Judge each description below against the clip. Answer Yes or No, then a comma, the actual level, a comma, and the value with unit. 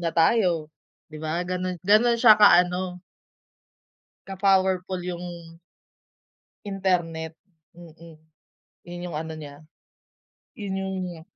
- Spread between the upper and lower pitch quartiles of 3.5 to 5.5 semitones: No, narrow, 2.5 semitones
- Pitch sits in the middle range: Yes, medium, 180 Hz